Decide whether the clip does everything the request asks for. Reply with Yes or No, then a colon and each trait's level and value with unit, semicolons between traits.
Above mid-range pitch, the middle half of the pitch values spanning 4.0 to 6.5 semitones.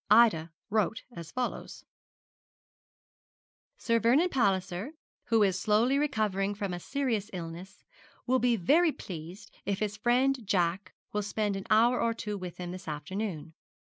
Yes: high, 210 Hz; average, 4.3 semitones